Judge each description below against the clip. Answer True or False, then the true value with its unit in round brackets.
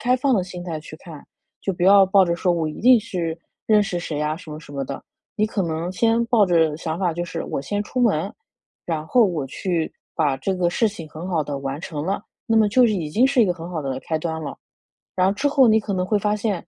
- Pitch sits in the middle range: True (180 Hz)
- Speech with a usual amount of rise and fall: True (4.7 semitones)